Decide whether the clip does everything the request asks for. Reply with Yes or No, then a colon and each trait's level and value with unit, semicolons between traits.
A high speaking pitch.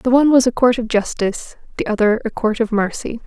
Yes: high, 230 Hz